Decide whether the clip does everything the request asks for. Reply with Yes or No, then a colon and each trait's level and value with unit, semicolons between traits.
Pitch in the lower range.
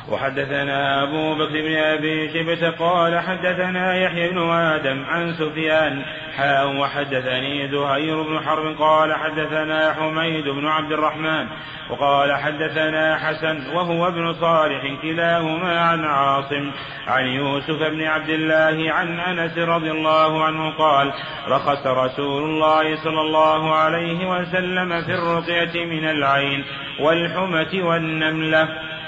No: medium, 155 Hz